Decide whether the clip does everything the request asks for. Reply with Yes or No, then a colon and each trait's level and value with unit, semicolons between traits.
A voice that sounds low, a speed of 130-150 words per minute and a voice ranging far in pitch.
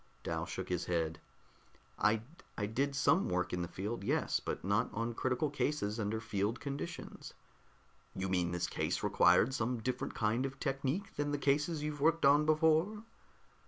No: low, 125 Hz; average, 170 wpm; wide, 6.2 semitones